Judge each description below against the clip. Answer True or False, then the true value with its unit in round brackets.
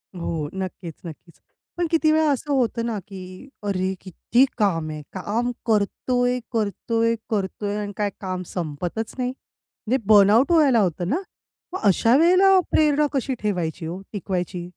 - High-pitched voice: True (210 Hz)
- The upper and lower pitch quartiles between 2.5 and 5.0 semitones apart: False (5.4 semitones)